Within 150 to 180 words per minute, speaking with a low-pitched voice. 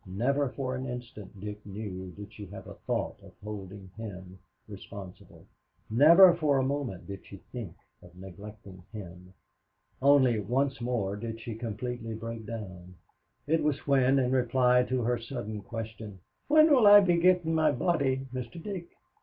Yes: average, 160 wpm; low, 115 Hz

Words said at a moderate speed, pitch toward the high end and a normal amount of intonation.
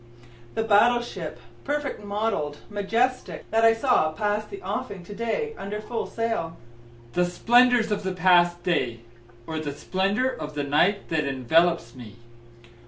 No: average, 145 wpm; high, 195 Hz; wide, 6.3 semitones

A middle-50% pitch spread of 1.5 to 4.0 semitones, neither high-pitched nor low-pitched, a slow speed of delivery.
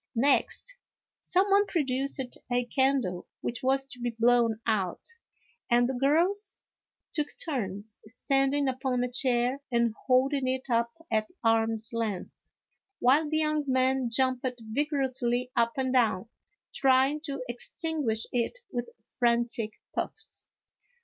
No: average, 2.7 semitones; very high, 255 Hz; slow, 130 wpm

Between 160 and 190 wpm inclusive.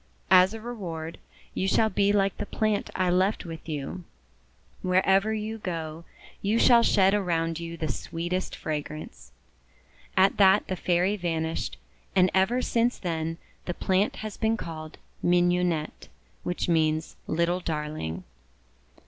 No: slow, 135 wpm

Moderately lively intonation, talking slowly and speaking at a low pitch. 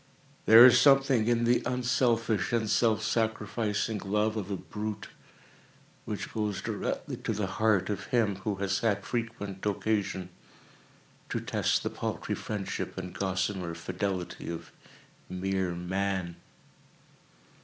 Yes: average, 3.0 semitones; slow, 125 wpm; low, 105 Hz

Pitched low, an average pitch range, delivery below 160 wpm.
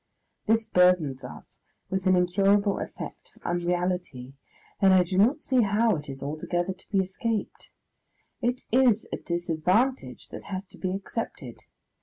No: medium, 185 Hz; average, 3.5 semitones; average, 150 wpm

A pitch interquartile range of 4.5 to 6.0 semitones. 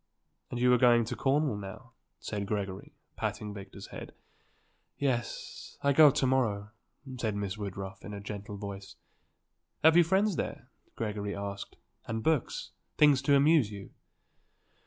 Yes: wide, 5.4 semitones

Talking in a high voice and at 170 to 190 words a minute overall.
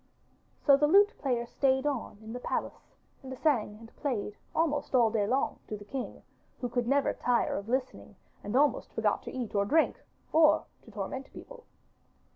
Yes: very high, 255 Hz; average, 180 wpm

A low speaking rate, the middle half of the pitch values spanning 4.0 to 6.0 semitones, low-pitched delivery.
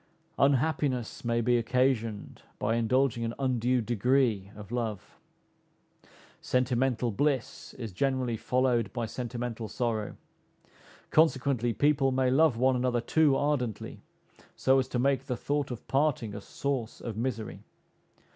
No: slow, 130 wpm; narrow, 2.6 semitones; low, 125 Hz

